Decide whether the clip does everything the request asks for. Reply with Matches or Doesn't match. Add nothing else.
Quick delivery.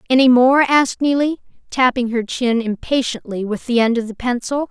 Doesn't match